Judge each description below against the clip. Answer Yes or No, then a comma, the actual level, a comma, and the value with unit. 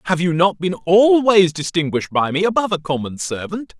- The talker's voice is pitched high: No, medium, 175 Hz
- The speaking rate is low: No, fast, 205 wpm